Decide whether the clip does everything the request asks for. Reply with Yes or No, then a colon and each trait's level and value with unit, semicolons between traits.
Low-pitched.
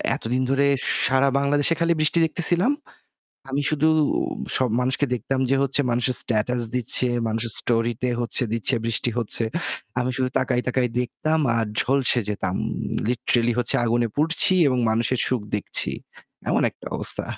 Yes: low, 125 Hz